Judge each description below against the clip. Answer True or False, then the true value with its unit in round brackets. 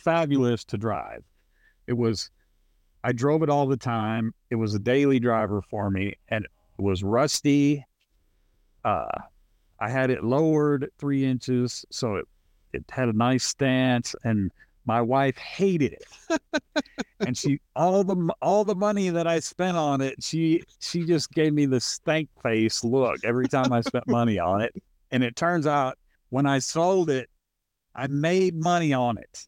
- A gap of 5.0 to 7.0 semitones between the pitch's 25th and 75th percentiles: True (5.3 semitones)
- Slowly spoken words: False (165 wpm)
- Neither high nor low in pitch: False (130 Hz)